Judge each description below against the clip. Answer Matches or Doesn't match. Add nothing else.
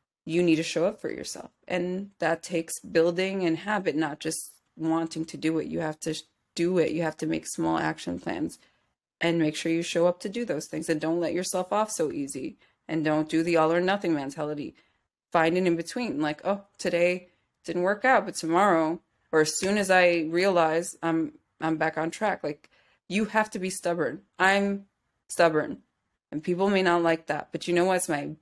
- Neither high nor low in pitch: Matches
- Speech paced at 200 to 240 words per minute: Matches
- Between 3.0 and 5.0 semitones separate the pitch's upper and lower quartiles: Doesn't match